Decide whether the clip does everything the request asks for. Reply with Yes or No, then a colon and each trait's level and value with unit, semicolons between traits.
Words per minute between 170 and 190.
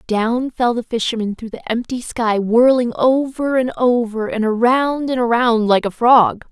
Yes: average, 175 wpm